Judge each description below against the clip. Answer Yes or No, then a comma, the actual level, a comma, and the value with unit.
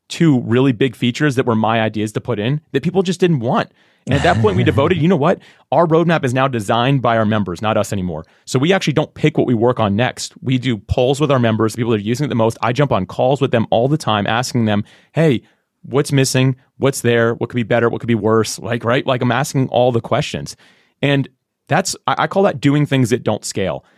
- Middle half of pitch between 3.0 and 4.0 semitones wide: Yes, average, 3.7 semitones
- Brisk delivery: Yes, fast, 255 wpm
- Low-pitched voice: Yes, low, 125 Hz